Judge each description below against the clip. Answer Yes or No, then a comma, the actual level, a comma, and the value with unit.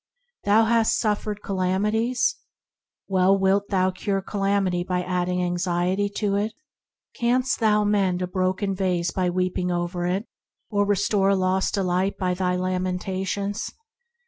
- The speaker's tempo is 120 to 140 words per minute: Yes, slow, 135 wpm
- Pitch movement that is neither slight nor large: No, narrow, 2.0 semitones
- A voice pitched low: No, high, 190 Hz